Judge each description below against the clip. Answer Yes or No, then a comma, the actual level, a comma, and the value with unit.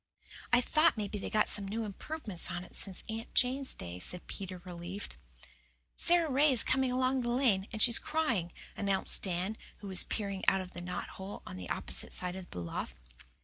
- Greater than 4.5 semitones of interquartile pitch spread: Yes, wide, 5.5 semitones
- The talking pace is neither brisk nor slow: Yes, average, 195 wpm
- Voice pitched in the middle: No, high, 205 Hz